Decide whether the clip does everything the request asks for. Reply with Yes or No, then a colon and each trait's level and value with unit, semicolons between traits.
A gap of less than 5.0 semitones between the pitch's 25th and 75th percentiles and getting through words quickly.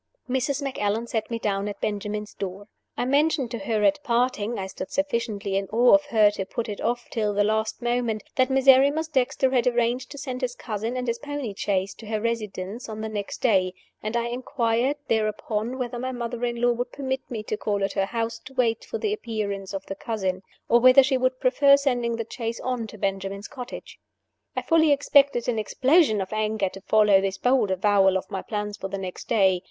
Yes: average, 3.6 semitones; fast, 210 wpm